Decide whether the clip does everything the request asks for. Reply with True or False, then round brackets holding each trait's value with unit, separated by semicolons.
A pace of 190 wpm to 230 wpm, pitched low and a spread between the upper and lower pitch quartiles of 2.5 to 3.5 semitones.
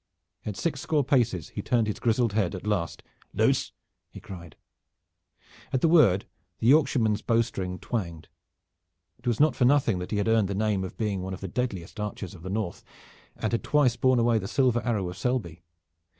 False (195 wpm; 110 Hz; 4.6 semitones)